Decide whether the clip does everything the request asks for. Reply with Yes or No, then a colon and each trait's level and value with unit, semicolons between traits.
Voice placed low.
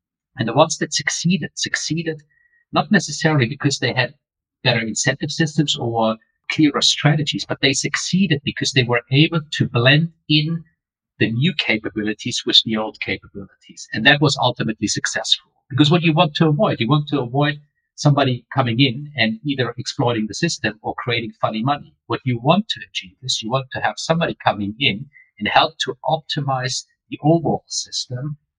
No: medium, 145 Hz